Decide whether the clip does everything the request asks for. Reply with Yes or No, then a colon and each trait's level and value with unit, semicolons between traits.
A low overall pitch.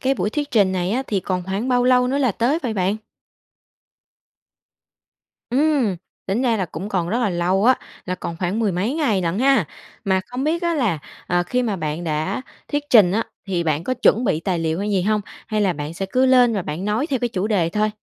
No: high, 210 Hz